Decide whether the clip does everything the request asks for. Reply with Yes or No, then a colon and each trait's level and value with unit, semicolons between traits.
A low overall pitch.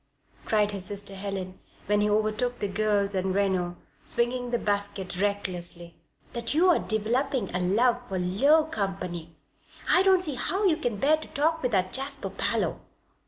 No: high, 210 Hz